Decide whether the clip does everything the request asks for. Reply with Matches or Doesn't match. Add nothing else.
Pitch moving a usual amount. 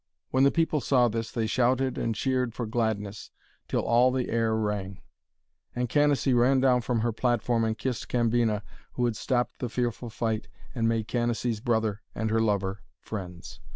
Doesn't match